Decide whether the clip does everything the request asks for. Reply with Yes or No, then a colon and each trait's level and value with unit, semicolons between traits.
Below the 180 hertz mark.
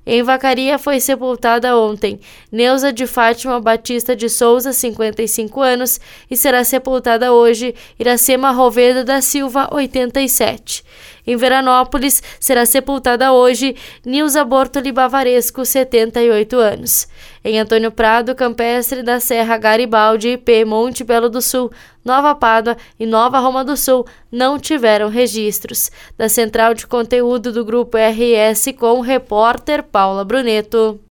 No: high, 245 Hz